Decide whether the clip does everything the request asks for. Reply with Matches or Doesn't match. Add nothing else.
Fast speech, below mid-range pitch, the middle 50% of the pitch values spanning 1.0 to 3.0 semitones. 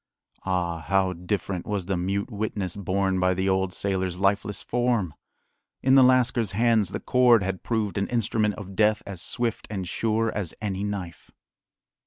Doesn't match